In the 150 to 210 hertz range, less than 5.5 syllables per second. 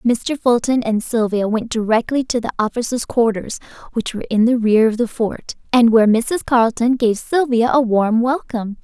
No: high, 235 Hz; 5.1 syllables/s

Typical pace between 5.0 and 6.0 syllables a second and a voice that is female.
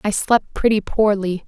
No: 4.4 syllables/s; female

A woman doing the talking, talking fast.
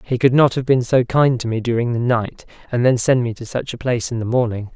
No: male; fast, 290 wpm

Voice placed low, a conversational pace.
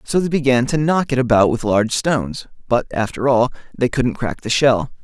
No: low, 125 Hz; fast, 215 wpm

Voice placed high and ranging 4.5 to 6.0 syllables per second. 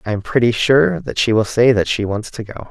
No: low, 115 Hz; 5.7 syllables/s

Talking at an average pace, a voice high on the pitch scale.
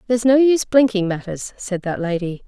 Yes: average, 195 wpm; high, 210 Hz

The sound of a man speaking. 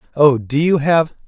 Yes: male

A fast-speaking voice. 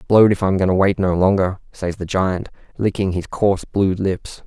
Yes: fast, 215 wpm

